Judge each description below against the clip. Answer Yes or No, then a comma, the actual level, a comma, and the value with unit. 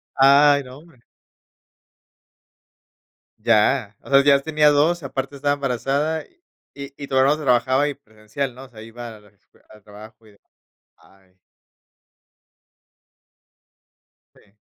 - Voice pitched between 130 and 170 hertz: Yes, low, 135 Hz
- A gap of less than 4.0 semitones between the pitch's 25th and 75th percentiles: No, average, 4.3 semitones